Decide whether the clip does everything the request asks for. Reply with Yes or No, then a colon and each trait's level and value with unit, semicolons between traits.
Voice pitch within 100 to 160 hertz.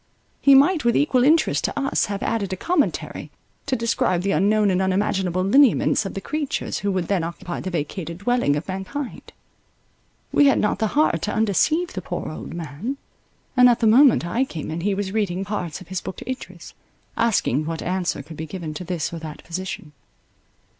No: high, 195 Hz